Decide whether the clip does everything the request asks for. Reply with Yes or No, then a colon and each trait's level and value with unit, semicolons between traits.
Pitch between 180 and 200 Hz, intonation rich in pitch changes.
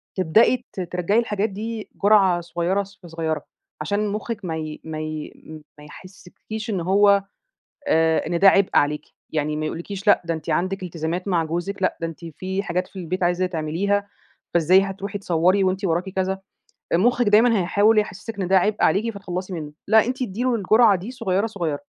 No: high, 190 Hz; average, 3.3 semitones